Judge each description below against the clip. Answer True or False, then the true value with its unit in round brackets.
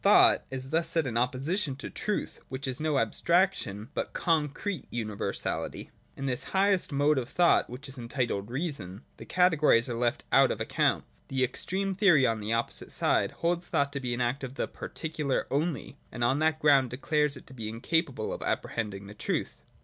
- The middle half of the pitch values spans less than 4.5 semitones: False (4.8 semitones)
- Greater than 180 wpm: True (195 wpm)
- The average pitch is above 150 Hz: False (135 Hz)